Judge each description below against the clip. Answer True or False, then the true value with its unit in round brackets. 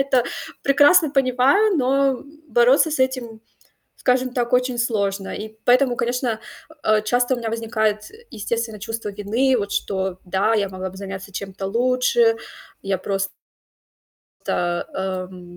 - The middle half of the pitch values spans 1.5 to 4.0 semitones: False (4.5 semitones)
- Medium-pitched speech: False (230 Hz)